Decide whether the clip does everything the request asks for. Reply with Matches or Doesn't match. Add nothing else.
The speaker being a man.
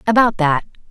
Doesn't match